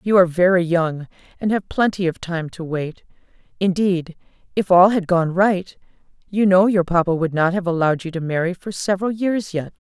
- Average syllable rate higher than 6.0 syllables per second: No, 5.3 syllables/s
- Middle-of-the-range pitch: Yes, medium, 180 Hz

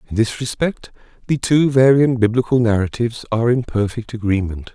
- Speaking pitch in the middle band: No, low, 120 Hz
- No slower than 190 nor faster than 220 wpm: No, average, 150 wpm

